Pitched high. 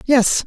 Yes: very high, 255 Hz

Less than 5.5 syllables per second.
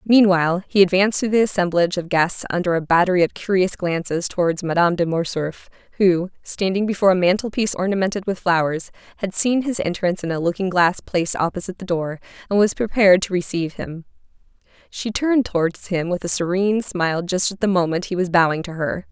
No: 6.1 syllables/s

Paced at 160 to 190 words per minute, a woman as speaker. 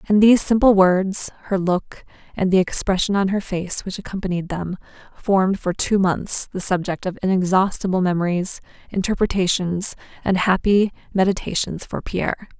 No: average, 145 wpm; female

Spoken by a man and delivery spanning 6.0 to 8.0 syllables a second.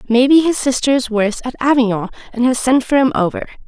No: female; 6.3 syllables/s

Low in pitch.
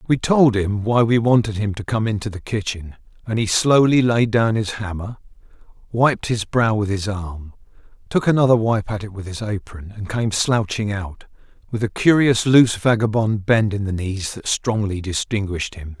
Yes: low, 110 Hz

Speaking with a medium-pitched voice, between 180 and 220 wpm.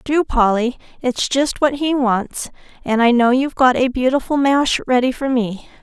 No: very high, 255 Hz; average, 185 wpm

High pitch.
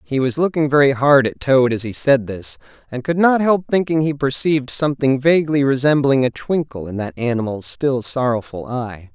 No: low, 135 Hz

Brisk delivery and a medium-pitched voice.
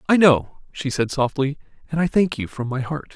Yes: fast, 230 wpm; medium, 145 Hz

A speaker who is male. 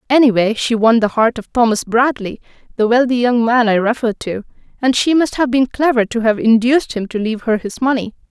No: female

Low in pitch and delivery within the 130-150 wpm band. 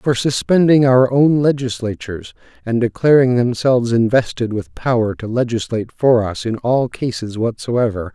Yes: low, 120 Hz; average, 140 wpm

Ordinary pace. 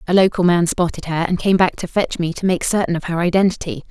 No: fast, 260 wpm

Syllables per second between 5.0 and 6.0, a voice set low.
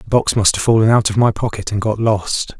Yes: 5.5 syllables/s; low, 105 Hz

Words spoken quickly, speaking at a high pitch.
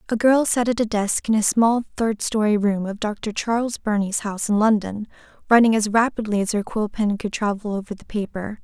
Yes: fast, 215 wpm; high, 215 Hz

